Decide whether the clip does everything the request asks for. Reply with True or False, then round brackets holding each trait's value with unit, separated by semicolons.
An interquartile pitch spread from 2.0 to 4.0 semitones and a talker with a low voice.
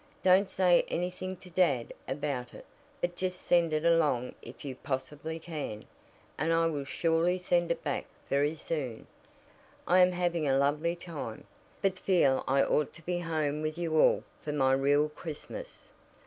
False (3.6 semitones; 160 Hz)